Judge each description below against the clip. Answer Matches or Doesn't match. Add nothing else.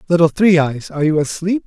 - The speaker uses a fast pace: Matches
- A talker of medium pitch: Matches